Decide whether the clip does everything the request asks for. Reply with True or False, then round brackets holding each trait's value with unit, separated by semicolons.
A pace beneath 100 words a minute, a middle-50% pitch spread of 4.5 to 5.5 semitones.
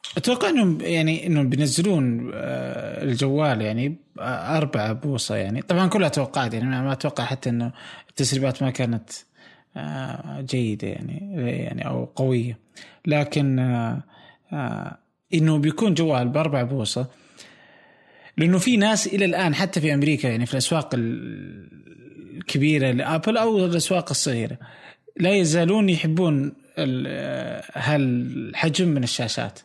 False (105 wpm; 5.0 semitones)